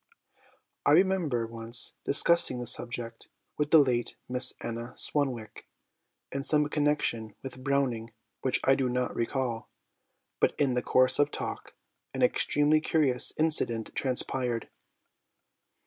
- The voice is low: Yes, low, 130 Hz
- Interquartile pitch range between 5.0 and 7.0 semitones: No, average, 3.6 semitones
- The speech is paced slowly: Yes, slow, 125 wpm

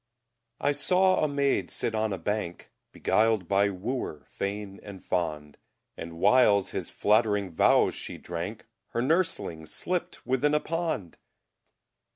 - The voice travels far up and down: Yes, wide, 6.9 semitones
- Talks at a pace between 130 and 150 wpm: Yes, slow, 135 wpm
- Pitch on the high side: No, low, 105 Hz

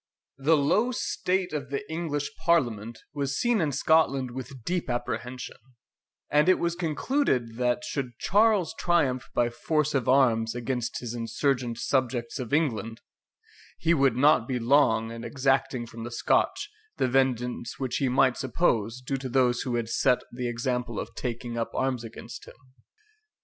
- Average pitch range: Yes, average, 3.7 semitones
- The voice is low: Yes, low, 130 Hz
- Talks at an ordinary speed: Yes, average, 160 wpm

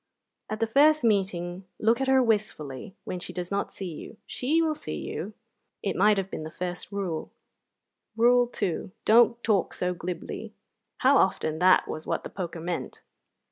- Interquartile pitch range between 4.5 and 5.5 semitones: Yes, average, 4.9 semitones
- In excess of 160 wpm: Yes, average, 170 wpm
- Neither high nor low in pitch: No, high, 200 Hz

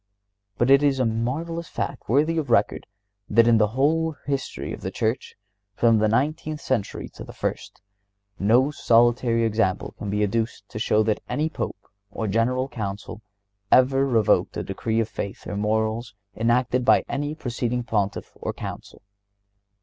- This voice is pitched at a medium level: No, low, 115 Hz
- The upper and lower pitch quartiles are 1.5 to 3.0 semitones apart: No, average, 3.7 semitones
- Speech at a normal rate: Yes, average, 160 wpm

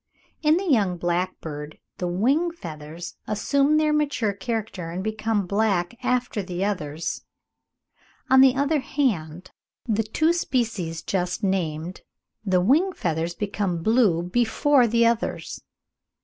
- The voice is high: Yes, high, 205 Hz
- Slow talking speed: Yes, slow, 130 wpm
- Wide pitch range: Yes, wide, 6.3 semitones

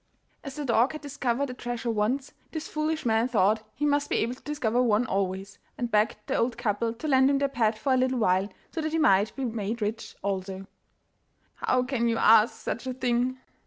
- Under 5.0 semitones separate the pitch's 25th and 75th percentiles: Yes, average, 3.7 semitones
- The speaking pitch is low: No, high, 240 Hz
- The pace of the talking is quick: Yes, fast, 215 wpm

